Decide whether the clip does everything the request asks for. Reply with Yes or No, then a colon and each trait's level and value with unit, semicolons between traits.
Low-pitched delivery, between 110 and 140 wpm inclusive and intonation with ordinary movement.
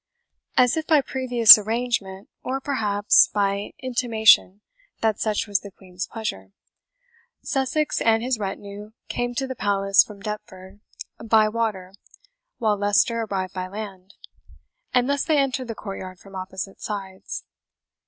No: high, 210 Hz; slow, 135 wpm; average, 3.7 semitones